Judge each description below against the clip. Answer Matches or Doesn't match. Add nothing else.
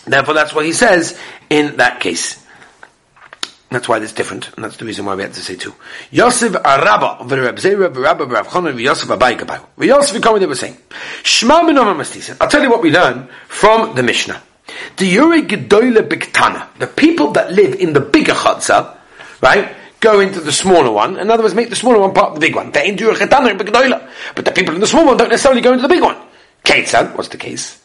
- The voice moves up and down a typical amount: Doesn't match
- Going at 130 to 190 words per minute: Doesn't match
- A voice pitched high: Matches